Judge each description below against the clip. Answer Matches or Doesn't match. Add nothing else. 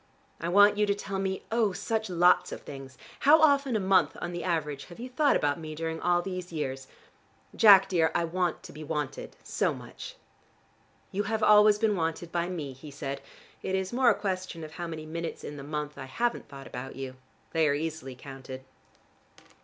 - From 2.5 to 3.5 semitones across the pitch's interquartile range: Doesn't match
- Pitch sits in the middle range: Matches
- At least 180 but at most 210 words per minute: Matches